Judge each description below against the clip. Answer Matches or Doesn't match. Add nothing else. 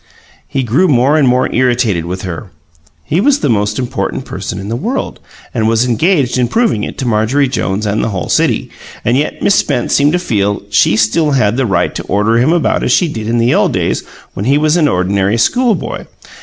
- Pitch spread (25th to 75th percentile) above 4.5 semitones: Matches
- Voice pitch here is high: Doesn't match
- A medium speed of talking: Doesn't match